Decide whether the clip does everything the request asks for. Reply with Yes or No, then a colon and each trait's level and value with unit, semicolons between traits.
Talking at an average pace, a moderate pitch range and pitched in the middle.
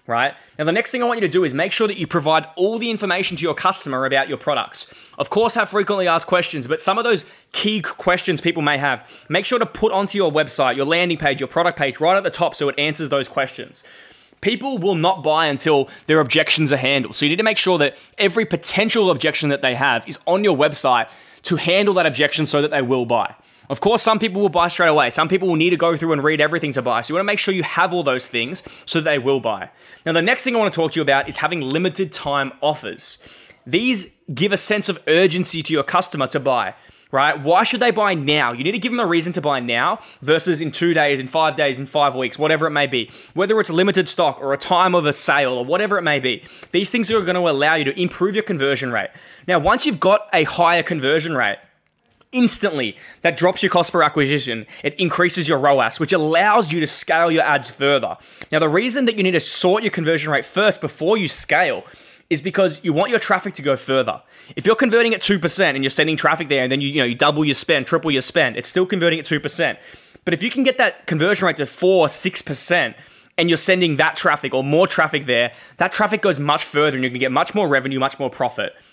No: fast, 250 wpm; average, 4.8 semitones; medium, 165 Hz